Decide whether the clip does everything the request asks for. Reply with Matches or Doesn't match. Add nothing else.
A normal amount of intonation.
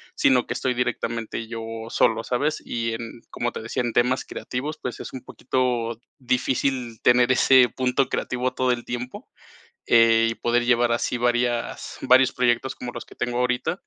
Doesn't match